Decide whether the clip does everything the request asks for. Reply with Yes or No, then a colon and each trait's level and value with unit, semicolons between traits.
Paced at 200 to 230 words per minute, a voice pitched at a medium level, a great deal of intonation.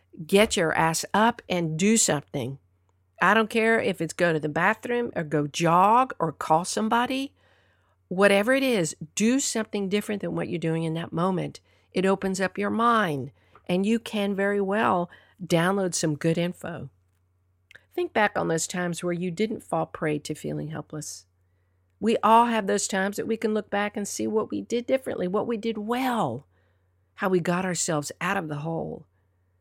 No: average, 180 wpm; medium, 175 Hz; wide, 6.1 semitones